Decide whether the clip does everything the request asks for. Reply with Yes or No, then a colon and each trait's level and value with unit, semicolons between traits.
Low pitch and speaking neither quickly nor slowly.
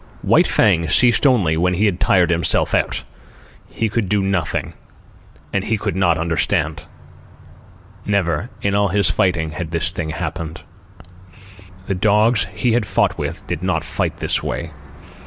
Yes: very low, 90 Hz; average, 155 wpm